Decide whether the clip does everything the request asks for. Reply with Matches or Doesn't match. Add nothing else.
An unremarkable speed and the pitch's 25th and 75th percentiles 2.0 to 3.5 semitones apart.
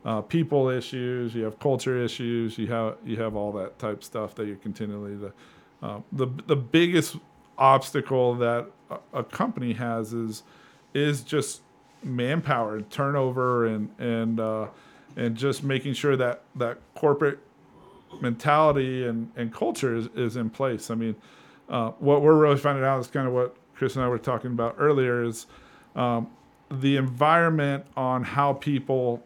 Matches